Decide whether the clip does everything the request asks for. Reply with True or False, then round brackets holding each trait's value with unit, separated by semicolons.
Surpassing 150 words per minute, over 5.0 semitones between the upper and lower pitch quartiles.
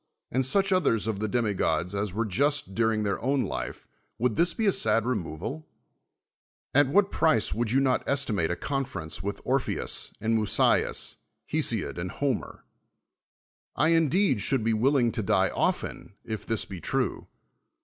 True (160 wpm; 5.4 semitones)